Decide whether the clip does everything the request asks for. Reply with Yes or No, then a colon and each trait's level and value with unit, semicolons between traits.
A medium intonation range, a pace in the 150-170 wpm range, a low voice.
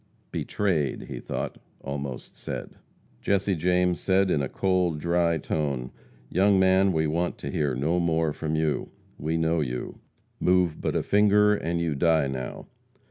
Yes: average, 3.6 semitones; average, 155 wpm; very low, 85 Hz